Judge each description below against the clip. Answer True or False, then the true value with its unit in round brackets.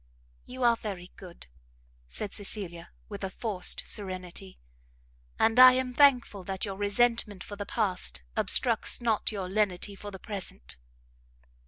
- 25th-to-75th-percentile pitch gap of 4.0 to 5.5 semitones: False (3.4 semitones)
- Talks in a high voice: True (205 Hz)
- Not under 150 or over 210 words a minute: False (140 wpm)